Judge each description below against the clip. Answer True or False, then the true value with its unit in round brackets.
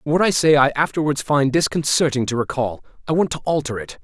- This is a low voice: False (145 Hz)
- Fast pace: True (210 wpm)